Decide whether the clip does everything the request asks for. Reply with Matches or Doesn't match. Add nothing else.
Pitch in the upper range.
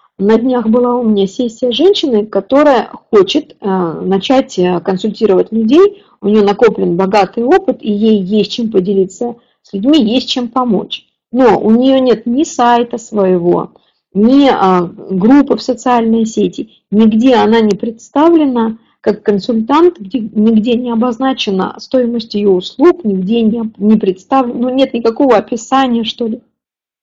Matches